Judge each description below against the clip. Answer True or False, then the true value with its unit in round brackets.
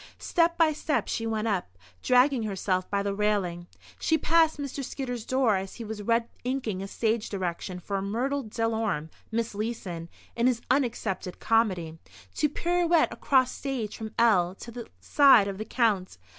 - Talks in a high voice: True (225 Hz)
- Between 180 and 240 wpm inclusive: False (165 wpm)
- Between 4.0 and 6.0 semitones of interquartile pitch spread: True (4.7 semitones)